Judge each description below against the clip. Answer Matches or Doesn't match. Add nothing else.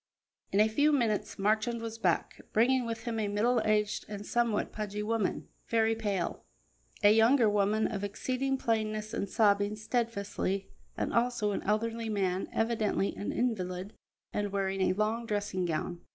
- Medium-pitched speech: Doesn't match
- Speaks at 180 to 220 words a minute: Doesn't match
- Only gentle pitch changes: Matches